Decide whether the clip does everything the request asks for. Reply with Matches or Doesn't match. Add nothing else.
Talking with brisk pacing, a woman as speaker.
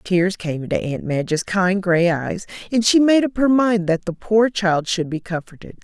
Matches